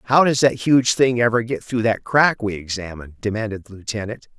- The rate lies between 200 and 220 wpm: Yes, fast, 205 wpm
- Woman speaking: No, male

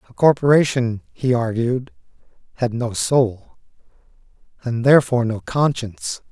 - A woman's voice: No, male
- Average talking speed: No, slow, 105 wpm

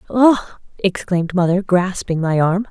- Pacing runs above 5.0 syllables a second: No, 4.6 syllables/s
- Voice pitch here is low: No, medium, 185 Hz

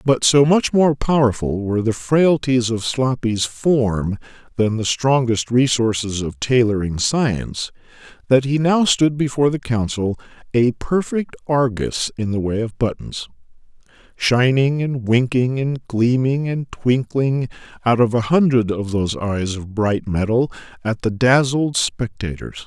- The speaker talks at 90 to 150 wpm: Yes, average, 145 wpm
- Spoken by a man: Yes, male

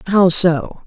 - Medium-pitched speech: Yes, medium, 175 Hz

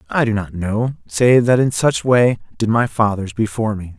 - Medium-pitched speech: No, low, 110 Hz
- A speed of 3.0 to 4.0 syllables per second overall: No, 4.9 syllables/s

